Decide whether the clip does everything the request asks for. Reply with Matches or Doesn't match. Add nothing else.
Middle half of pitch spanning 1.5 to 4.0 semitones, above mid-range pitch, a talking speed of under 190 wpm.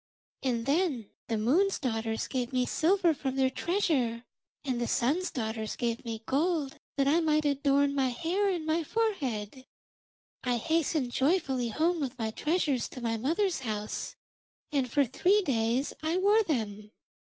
Doesn't match